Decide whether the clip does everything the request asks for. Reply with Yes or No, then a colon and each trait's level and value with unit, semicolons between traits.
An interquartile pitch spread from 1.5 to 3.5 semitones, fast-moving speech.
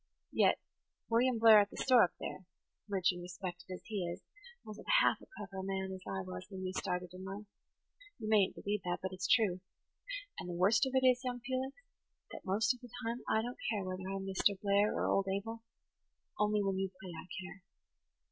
Yes: average, 3.2 semitones; fast, 210 wpm